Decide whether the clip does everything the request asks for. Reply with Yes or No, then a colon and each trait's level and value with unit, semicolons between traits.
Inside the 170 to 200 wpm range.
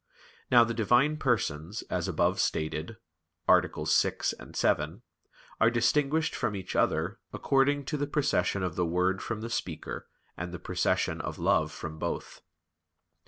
No: average, 145 wpm